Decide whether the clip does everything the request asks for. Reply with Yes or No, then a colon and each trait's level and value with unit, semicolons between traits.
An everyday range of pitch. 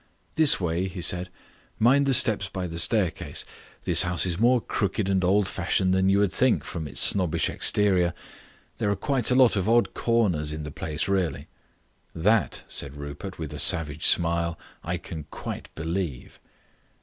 Yes: average, 4.0 semitones